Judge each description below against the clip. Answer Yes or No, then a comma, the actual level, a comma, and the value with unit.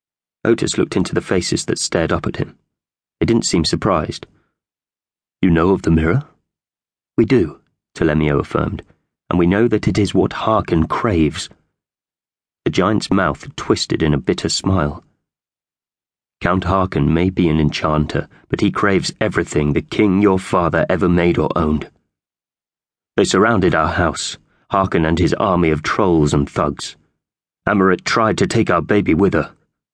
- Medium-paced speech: Yes, average, 155 wpm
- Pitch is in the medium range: No, very low, 85 Hz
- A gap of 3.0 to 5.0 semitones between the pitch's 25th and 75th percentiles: Yes, average, 3.6 semitones